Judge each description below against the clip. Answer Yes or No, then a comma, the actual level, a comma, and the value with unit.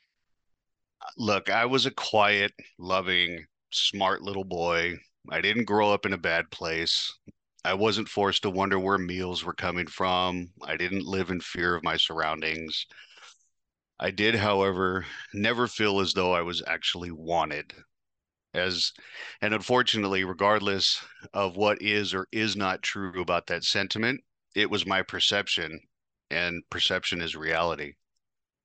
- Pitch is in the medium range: No, very low, 95 Hz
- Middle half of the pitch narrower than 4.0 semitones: Yes, average, 2.7 semitones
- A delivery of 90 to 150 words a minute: Yes, average, 140 wpm